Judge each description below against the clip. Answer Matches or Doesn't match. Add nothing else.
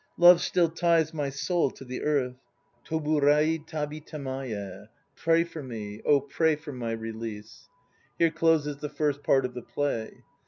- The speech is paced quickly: Doesn't match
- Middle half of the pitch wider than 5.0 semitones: Doesn't match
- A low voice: Doesn't match